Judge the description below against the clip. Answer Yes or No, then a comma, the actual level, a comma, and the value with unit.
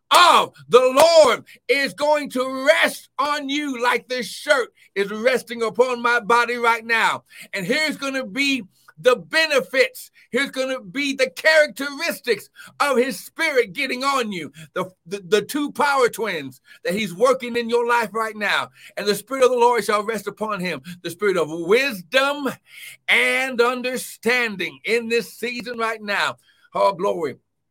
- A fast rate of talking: No, average, 165 wpm